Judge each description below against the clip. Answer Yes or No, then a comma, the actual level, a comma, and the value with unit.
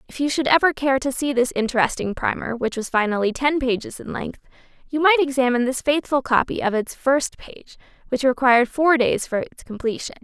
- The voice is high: Yes, very high, 265 Hz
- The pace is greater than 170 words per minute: Yes, average, 200 wpm